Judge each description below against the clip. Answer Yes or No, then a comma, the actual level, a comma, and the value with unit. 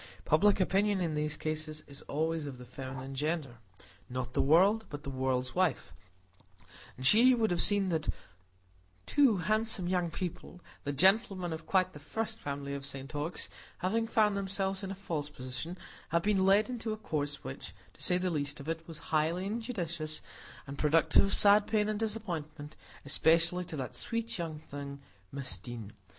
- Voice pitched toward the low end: No, medium, 165 Hz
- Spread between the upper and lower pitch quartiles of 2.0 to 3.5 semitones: No, wide, 5.5 semitones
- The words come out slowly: No, average, 165 wpm